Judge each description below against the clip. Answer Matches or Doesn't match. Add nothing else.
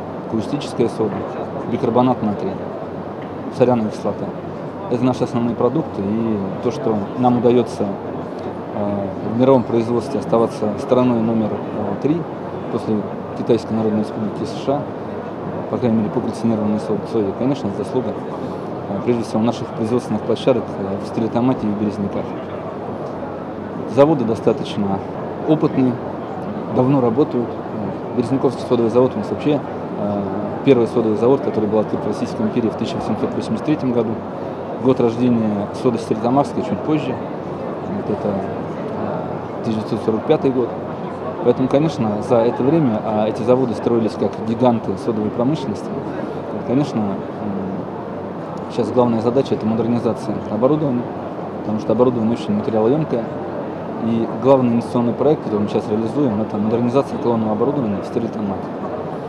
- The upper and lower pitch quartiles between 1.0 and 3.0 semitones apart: Matches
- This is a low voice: Matches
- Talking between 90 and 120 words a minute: Matches